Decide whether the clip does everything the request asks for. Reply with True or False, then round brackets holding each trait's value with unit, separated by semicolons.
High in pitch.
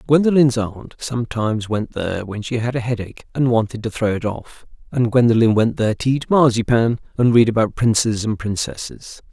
False (115 Hz)